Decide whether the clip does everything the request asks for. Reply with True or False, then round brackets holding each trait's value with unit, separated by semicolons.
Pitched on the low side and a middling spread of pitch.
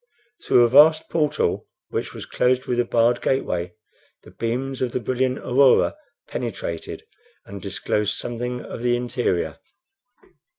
False (120 Hz; 2.1 semitones)